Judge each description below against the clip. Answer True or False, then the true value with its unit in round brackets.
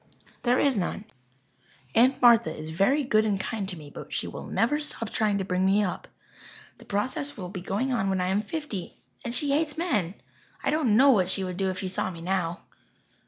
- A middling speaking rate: False (215 wpm)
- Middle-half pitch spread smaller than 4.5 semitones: False (5.5 semitones)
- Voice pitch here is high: True (205 Hz)